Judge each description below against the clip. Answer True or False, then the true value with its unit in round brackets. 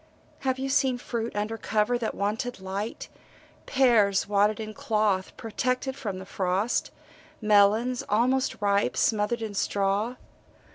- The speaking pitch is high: True (215 Hz)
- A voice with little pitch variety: False (3.3 semitones)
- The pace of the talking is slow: True (130 wpm)